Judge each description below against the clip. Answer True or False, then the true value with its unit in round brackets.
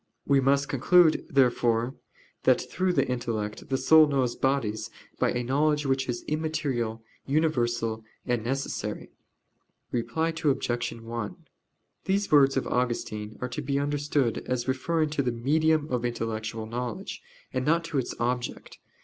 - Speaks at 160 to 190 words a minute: False (140 wpm)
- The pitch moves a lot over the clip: False (3.8 semitones)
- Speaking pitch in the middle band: False (130 Hz)